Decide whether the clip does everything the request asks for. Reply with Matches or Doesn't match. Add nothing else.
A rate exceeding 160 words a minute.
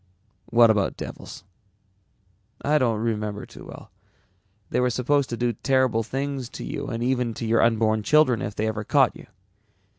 Matches